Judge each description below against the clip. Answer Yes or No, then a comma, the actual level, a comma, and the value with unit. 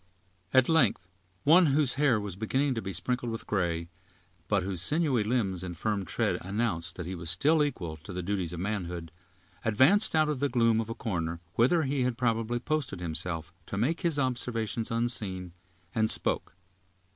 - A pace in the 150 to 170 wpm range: No, average, 180 wpm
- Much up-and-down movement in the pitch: Yes, wide, 6.3 semitones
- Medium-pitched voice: No, low, 110 Hz